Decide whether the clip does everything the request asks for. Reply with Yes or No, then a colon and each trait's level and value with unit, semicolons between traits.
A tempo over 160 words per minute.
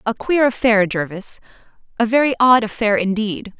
No: average, 150 wpm